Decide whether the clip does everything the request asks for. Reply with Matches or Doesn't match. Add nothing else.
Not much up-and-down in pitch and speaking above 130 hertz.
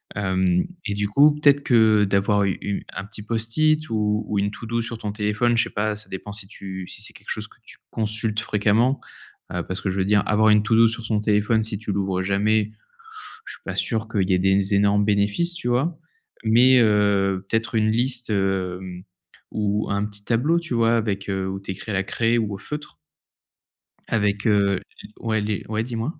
Doesn't match